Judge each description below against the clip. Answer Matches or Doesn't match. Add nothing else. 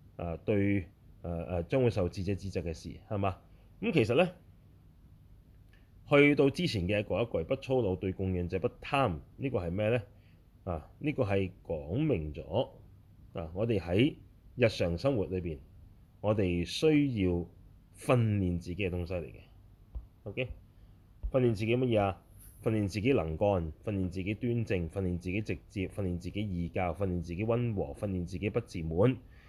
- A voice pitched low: Matches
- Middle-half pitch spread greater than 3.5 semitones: Doesn't match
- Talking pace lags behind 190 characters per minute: Doesn't match